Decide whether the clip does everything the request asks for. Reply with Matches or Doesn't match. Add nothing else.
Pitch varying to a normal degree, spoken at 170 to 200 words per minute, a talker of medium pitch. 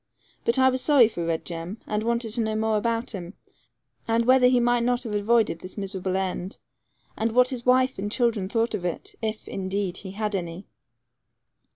Doesn't match